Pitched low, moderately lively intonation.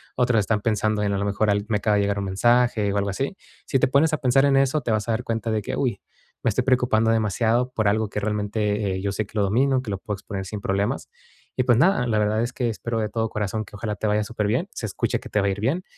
Yes: low, 110 Hz; average, 3.1 semitones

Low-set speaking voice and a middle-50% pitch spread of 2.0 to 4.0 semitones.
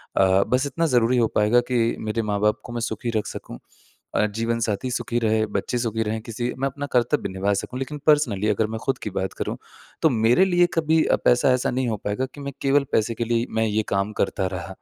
Yes: low, 115 Hz; average, 3.3 semitones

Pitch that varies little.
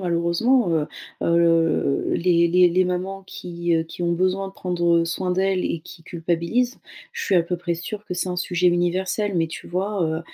Yes: narrow, 1.8 semitones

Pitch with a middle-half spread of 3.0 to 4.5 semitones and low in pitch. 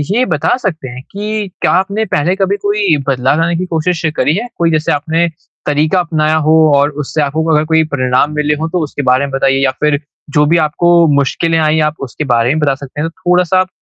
No: average, 3.5 semitones; medium, 155 Hz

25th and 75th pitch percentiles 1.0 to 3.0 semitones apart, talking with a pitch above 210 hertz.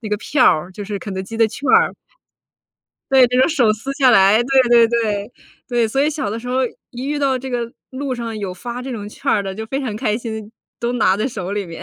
No: average, 3.6 semitones; high, 230 Hz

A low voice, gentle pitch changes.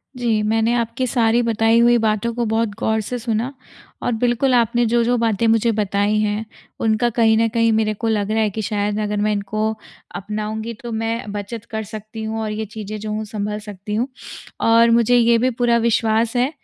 No: high, 220 Hz; narrow, 1.6 semitones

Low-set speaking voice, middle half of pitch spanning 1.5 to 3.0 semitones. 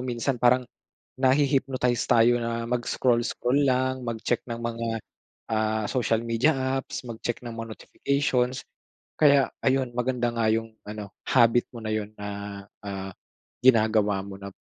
Yes: low, 120 Hz; average, 2.7 semitones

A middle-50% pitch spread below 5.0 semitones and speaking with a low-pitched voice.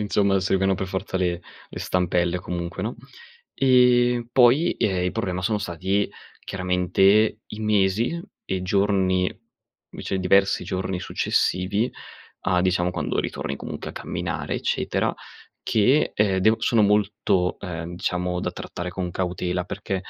Yes: narrow, 2.6 semitones; very low, 95 Hz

